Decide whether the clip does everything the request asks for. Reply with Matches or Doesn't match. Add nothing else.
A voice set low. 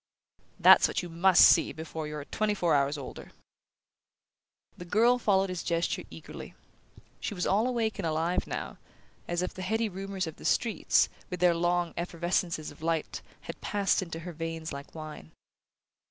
Doesn't match